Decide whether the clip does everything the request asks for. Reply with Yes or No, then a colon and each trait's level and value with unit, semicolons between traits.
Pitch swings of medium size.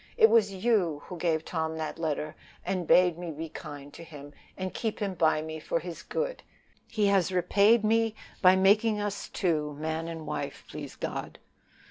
Yes: average, 4.4 semitones